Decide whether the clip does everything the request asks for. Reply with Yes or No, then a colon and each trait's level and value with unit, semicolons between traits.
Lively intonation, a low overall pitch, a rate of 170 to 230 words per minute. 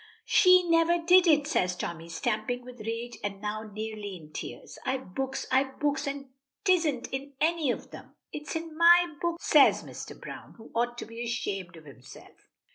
No: wide, 6.8 semitones; very high, 260 Hz; average, 185 wpm